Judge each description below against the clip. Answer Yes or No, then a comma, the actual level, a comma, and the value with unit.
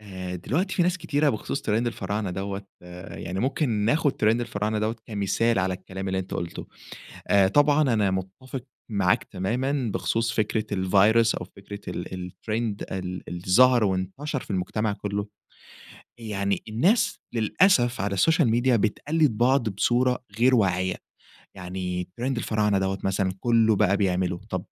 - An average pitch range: Yes, average, 4.1 semitones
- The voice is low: Yes, low, 105 Hz